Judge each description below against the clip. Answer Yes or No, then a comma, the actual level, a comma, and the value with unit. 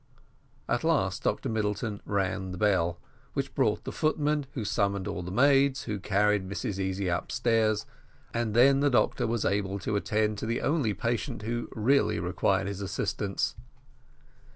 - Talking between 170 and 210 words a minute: No, average, 155 wpm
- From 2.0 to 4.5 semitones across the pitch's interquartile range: Yes, average, 3.2 semitones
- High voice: No, low, 105 Hz